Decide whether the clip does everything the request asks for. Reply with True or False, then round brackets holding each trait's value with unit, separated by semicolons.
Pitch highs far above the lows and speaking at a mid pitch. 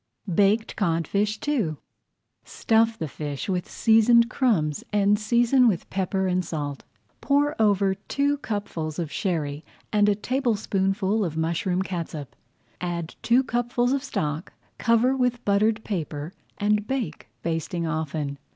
False (5.8 semitones; 200 Hz)